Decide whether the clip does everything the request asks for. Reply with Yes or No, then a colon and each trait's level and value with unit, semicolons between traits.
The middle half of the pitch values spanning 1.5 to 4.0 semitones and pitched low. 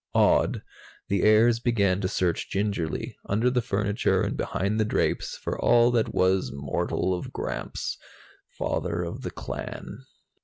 Yes: average, 3.4 semitones; low, 100 Hz